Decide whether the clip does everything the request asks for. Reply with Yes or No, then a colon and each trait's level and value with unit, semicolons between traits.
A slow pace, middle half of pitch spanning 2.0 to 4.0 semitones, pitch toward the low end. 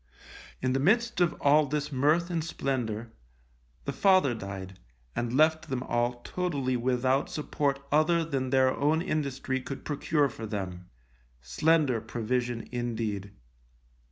No: slow, 130 wpm; average, 4.4 semitones; low, 130 Hz